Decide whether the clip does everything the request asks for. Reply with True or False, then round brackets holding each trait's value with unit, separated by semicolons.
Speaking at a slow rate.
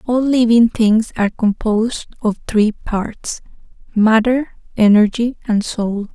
True (115 wpm)